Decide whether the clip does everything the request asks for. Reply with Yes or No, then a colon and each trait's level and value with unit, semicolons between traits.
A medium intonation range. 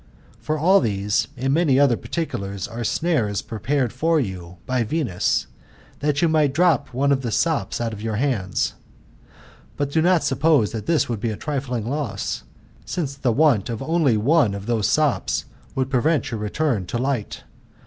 No: wide, 5.7 semitones